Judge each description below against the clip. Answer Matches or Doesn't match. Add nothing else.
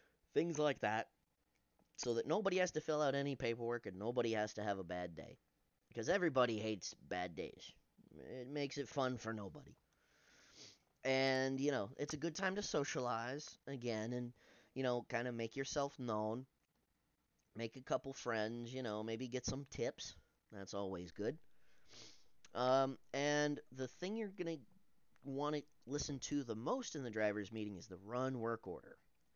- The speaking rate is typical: Matches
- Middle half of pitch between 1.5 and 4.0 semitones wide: Doesn't match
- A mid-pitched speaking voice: Doesn't match